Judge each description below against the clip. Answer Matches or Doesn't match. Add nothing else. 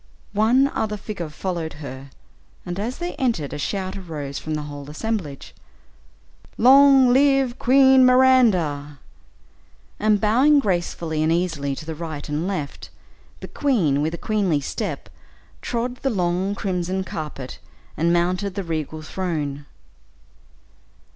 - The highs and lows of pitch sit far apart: Matches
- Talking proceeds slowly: Matches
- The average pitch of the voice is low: Doesn't match